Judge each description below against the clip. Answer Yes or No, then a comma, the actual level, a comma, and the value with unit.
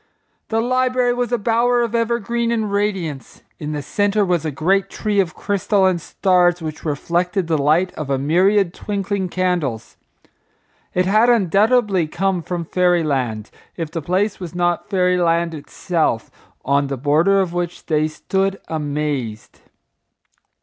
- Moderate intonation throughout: Yes, average, 4.5 semitones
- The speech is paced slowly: No, average, 150 wpm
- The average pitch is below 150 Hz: No, medium, 180 Hz